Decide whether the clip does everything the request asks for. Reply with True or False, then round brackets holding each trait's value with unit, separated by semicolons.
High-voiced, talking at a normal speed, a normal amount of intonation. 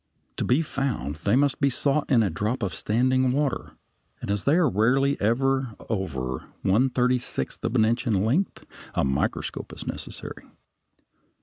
False (125 Hz; 170 wpm; 4.9 semitones)